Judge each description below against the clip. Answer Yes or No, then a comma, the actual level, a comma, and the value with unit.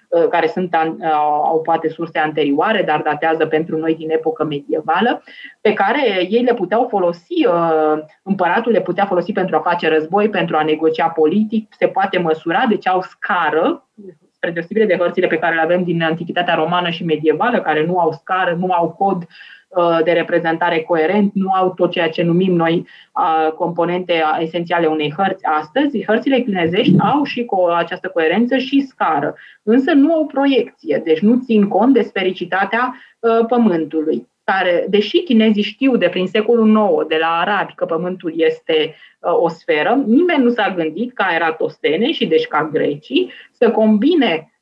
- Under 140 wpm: No, average, 165 wpm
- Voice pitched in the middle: Yes, medium, 180 Hz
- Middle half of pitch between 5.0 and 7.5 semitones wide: Yes, average, 5.3 semitones